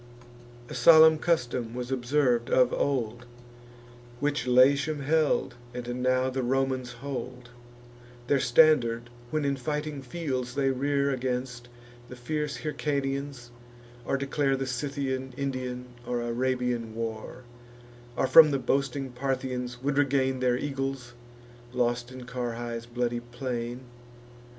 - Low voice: Yes, low, 130 Hz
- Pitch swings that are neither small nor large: No, narrow, 2.2 semitones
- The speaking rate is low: Yes, slow, 120 wpm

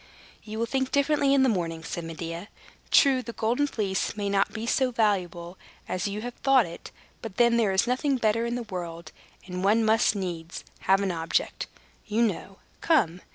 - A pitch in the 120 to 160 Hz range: No, high, 210 Hz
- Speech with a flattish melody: No, average, 4.9 semitones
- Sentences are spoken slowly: No, average, 190 wpm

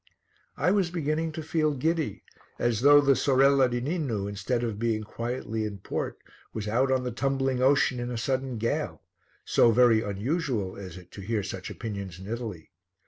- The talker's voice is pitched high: No, low, 120 Hz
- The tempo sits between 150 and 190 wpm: Yes, average, 180 wpm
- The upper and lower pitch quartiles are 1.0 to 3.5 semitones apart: No, average, 4.5 semitones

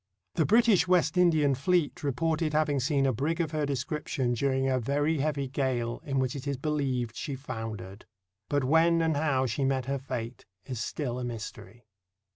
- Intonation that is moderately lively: Yes, average, 3.3 semitones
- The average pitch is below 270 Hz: Yes, medium, 140 Hz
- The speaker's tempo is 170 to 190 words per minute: Yes, average, 180 wpm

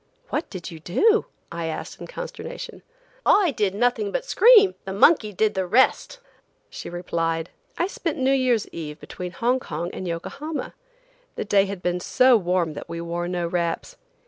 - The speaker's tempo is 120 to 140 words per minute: No, average, 170 wpm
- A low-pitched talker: No, high, 195 Hz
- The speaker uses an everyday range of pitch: No, wide, 7.9 semitones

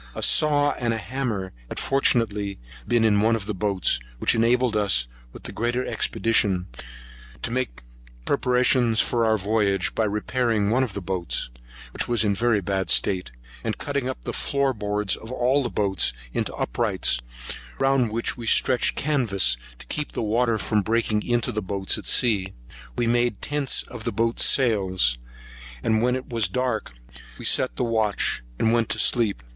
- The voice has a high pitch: No, low, 115 Hz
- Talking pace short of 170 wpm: No, average, 175 wpm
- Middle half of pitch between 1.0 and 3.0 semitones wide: No, average, 3.4 semitones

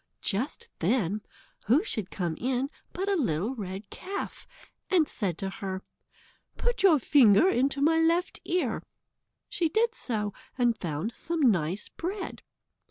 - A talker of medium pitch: No, high, 245 Hz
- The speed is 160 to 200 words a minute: No, average, 140 wpm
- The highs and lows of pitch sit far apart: Yes, wide, 8.8 semitones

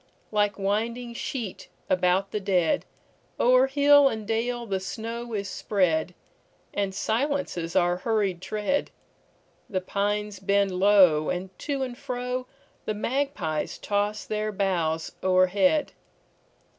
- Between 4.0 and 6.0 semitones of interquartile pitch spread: Yes, average, 4.3 semitones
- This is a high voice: Yes, high, 205 Hz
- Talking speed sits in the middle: No, slow, 105 wpm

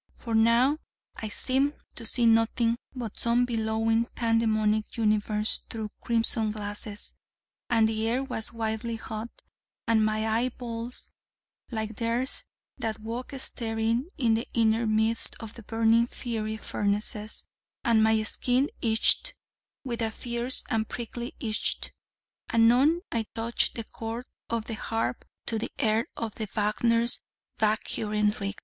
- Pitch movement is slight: Yes, narrow, 1.4 semitones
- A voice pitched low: No, high, 225 Hz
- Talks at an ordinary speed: No, slow, 130 wpm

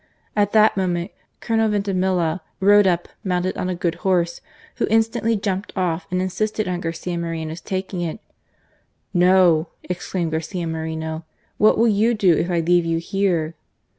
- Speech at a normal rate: Yes, average, 165 wpm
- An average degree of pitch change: Yes, average, 3.0 semitones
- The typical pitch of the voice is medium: Yes, medium, 180 Hz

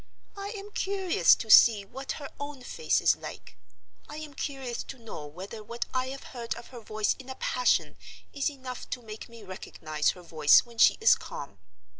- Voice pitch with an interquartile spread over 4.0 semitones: Yes, average, 4.8 semitones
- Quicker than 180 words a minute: Yes, average, 195 wpm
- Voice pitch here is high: Yes, high, 240 Hz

